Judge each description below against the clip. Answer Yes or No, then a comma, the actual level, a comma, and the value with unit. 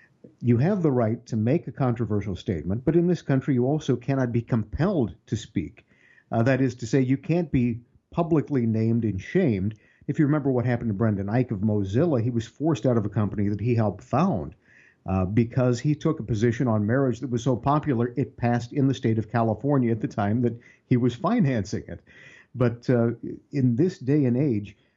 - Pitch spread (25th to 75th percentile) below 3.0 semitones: No, average, 3.4 semitones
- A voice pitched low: Yes, low, 120 Hz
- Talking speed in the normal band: No, fast, 210 wpm